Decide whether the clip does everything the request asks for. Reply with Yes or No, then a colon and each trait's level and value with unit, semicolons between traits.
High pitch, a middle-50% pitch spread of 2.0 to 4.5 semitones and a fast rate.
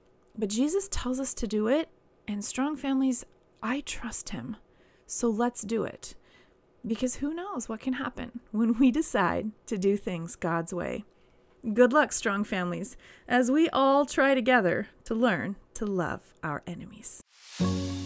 No: high, 240 Hz; average, 4.2 semitones; average, 155 wpm